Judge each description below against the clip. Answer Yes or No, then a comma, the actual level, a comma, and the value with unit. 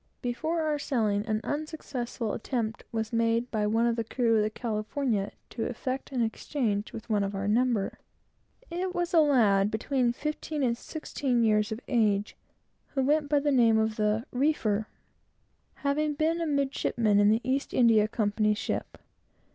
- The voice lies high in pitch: Yes, high, 235 Hz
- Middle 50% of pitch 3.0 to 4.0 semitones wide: No, average, 4.6 semitones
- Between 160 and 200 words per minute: Yes, average, 165 wpm